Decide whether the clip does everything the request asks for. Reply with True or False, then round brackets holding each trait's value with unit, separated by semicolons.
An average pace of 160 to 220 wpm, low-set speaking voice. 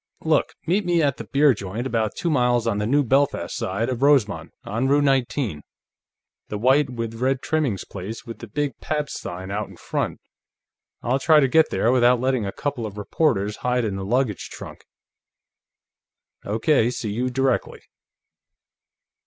True (170 wpm; 125 Hz)